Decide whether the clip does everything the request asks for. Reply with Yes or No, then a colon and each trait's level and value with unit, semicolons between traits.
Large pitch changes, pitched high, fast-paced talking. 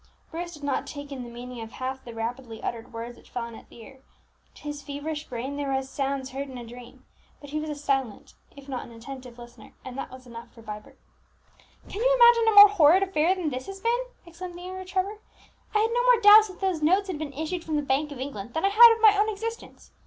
Yes: wide, 6.9 semitones; very high, 290 Hz; fast, 250 wpm